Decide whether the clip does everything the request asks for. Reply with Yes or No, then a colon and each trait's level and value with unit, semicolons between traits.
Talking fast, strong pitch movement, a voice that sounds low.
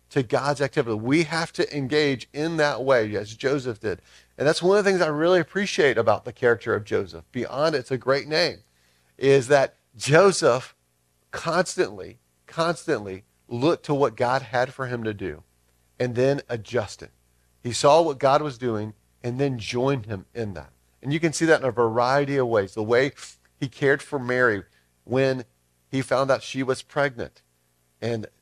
No: average, 180 wpm; wide, 7.1 semitones; low, 125 Hz